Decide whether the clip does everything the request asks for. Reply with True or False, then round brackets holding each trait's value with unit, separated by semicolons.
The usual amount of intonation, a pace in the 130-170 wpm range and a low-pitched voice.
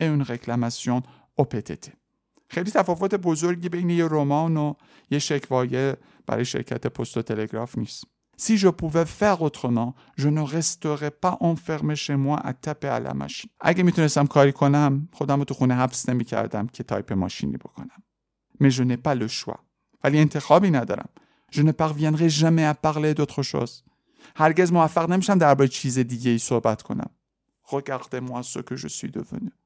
False (4.0 semitones; 155 wpm; 145 Hz)